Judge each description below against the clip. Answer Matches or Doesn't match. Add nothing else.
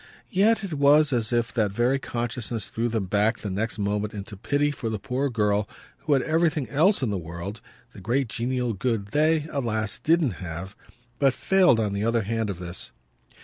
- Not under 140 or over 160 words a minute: Doesn't match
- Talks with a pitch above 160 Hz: Doesn't match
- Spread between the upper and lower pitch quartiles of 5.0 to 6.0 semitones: Matches